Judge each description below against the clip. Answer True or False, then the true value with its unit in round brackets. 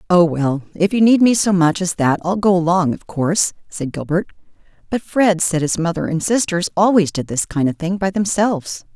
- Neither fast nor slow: False (215 wpm)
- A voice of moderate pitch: True (180 Hz)